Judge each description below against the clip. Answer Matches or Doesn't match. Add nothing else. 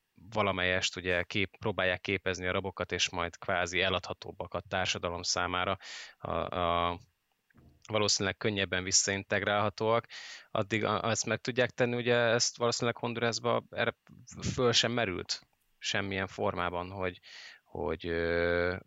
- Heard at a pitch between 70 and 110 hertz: Matches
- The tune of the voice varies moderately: Matches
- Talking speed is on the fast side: Doesn't match